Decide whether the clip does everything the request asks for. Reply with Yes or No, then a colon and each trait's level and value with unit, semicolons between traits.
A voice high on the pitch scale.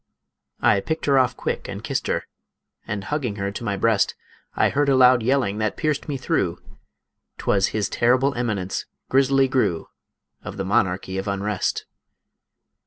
No: low, 110 Hz